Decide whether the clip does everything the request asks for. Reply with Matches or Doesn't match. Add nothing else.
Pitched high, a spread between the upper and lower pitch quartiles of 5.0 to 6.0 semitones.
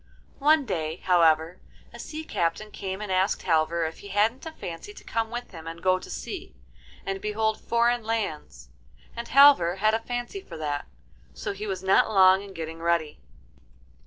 Matches